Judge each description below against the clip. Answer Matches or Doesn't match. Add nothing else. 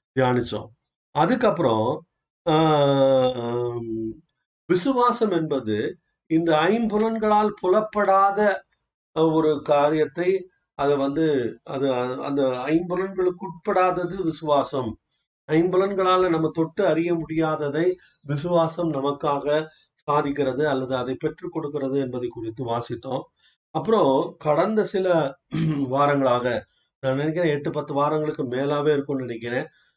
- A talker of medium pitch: Matches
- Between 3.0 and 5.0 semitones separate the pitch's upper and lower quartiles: Matches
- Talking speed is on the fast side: Doesn't match